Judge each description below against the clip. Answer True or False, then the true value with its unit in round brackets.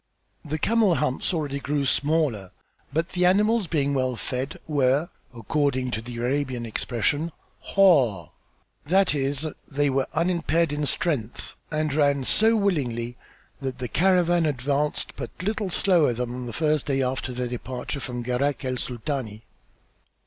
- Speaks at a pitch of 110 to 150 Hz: True (140 Hz)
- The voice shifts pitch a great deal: False (4.4 semitones)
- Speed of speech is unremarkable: True (145 wpm)